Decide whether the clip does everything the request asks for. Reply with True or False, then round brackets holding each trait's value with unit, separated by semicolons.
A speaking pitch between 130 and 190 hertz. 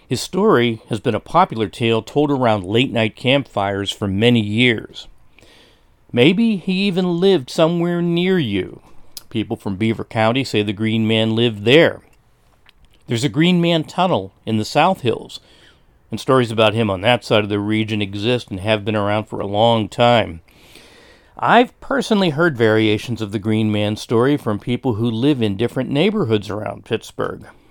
False (115 Hz)